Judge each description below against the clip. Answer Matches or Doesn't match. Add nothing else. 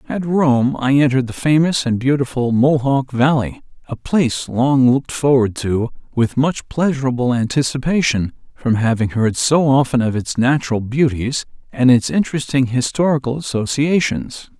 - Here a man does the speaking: Matches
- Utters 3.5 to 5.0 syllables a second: Matches